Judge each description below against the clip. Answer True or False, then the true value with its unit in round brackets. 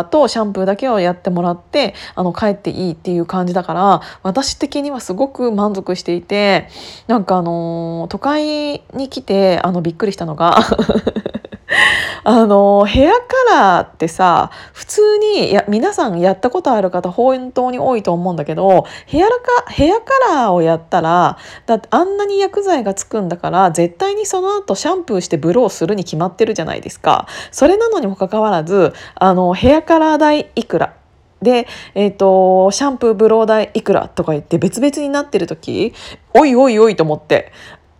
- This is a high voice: True (215 Hz)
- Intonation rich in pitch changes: True (7.6 semitones)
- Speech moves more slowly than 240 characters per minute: False (355 characters per minute)